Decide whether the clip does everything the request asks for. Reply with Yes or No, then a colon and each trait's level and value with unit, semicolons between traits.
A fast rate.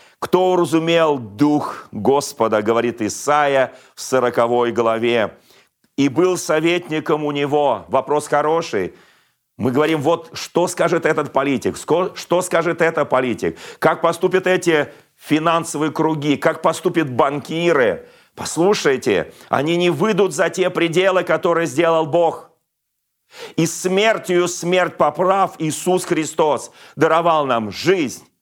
No: average, 115 wpm